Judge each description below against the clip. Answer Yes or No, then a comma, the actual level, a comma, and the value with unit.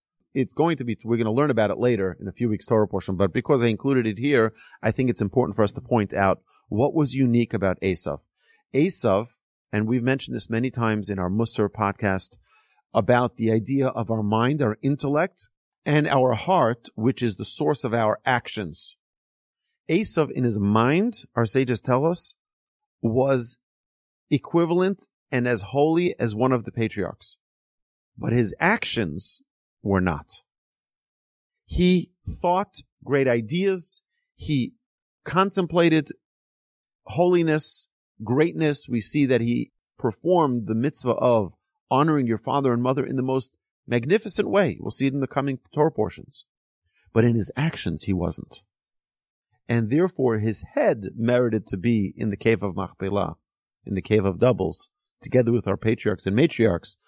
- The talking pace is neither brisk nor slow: Yes, average, 160 wpm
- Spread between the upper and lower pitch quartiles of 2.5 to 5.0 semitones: No, wide, 5.4 semitones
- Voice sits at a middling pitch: No, low, 120 Hz